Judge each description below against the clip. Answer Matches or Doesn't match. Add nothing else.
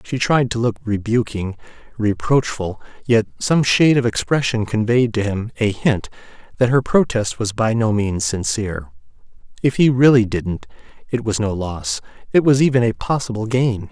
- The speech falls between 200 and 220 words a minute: Doesn't match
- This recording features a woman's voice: Doesn't match